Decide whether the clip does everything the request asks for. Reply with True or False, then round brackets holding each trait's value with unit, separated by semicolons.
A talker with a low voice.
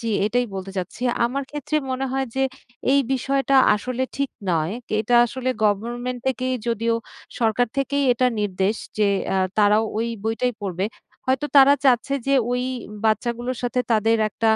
False (240 Hz)